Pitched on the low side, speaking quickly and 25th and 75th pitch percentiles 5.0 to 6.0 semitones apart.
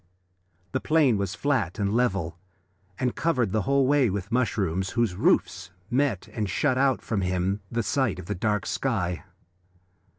No: low, 110 Hz; average, 165 wpm; wide, 5.5 semitones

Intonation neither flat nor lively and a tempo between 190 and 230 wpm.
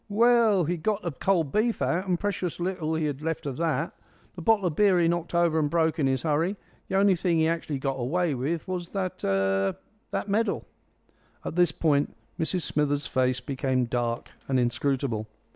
Yes: average, 4.9 semitones; average, 195 wpm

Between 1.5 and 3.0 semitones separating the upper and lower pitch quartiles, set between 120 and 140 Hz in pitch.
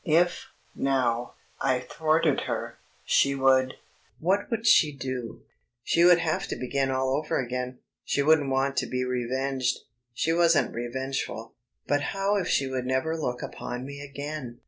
No: average, 3.6 semitones; low, 135 Hz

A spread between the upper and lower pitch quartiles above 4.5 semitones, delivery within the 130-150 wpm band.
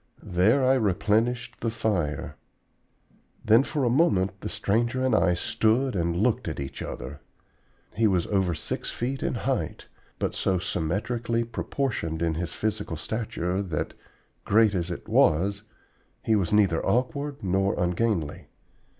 Yes: average, 5.0 semitones; average, 140 wpm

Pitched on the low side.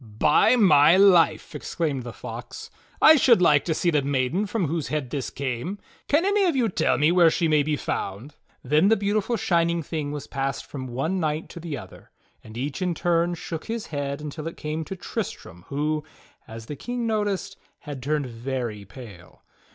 No: medium, 155 Hz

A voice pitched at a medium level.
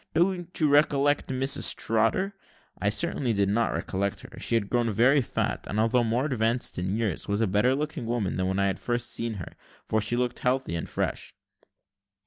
No: low, 115 Hz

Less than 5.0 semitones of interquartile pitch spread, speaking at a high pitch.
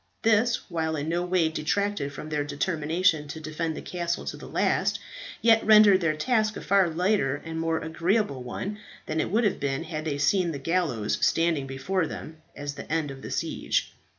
No: average, 4.1 semitones; medium, 165 Hz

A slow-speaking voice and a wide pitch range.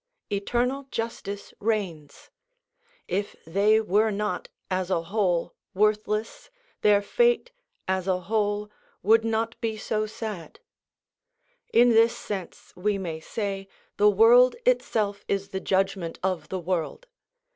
No: slow, 125 wpm; average, 2.9 semitones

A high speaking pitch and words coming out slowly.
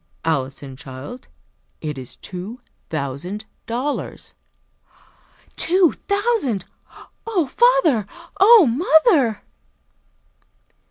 Yes: high, 240 Hz; slow, 70 wpm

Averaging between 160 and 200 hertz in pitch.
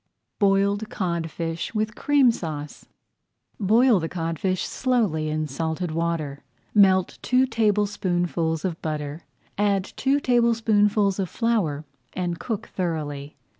Yes: medium, 185 Hz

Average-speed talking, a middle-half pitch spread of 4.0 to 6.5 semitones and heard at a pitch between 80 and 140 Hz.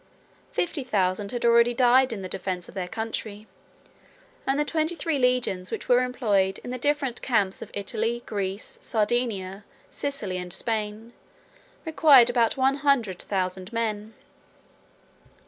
No: average, 145 wpm; average, 4.3 semitones; high, 230 Hz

